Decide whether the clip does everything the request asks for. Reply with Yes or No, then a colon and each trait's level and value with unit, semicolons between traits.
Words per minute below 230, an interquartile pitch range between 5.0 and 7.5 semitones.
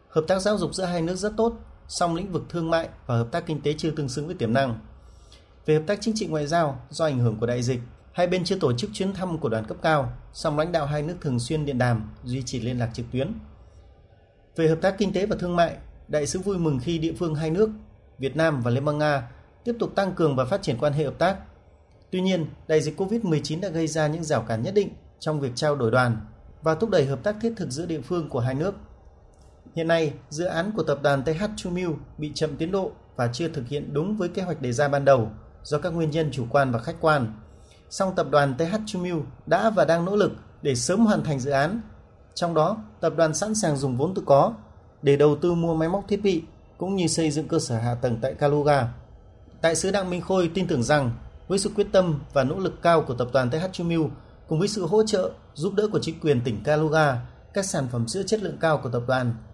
No: fast, 250 wpm; wide, 5.4 semitones